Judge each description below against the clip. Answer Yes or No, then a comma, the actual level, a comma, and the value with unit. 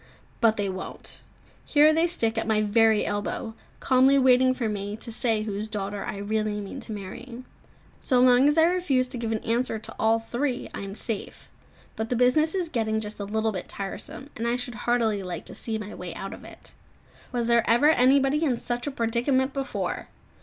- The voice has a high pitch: Yes, high, 230 Hz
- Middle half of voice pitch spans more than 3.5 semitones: No, average, 3.2 semitones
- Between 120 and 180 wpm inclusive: No, fast, 205 wpm